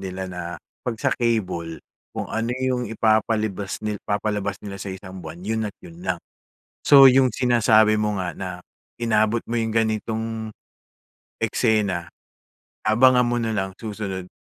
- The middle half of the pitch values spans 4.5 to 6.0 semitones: No, average, 3.0 semitones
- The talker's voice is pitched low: Yes, low, 110 Hz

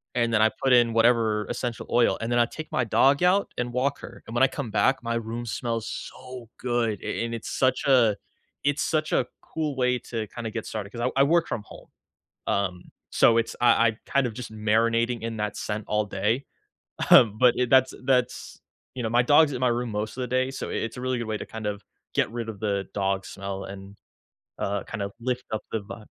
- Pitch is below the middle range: Yes, low, 115 Hz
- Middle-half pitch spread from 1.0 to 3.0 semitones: Yes, average, 2.7 semitones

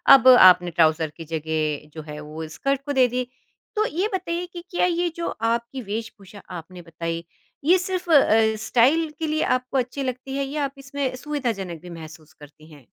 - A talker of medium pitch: No, high, 230 Hz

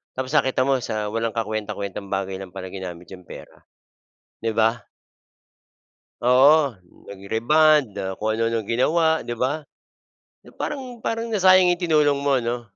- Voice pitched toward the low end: Yes, low, 120 Hz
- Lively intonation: Yes, wide, 6.4 semitones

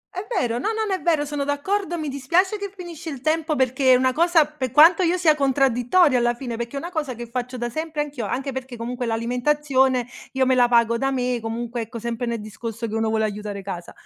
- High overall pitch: Yes, very high, 260 Hz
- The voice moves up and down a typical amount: Yes, average, 4.5 semitones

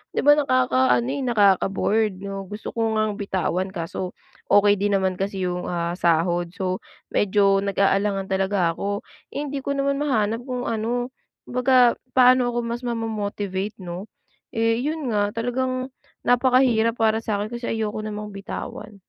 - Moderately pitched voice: No, high, 215 Hz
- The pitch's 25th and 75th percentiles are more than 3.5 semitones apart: Yes, average, 3.9 semitones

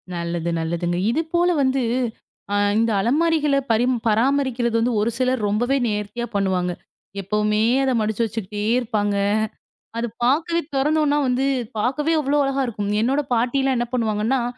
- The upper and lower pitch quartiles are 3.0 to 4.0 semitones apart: No, average, 4.4 semitones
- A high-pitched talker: Yes, high, 240 Hz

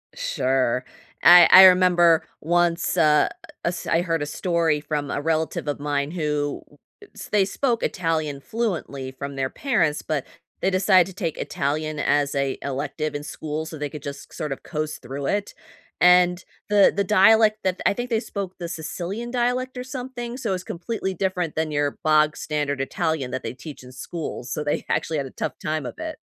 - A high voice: No, medium, 160 Hz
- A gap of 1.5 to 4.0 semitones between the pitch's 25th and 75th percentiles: No, average, 4.4 semitones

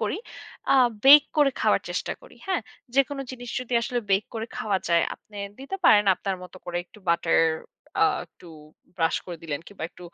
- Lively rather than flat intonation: Yes, wide, 7.3 semitones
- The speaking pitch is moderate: No, high, 210 Hz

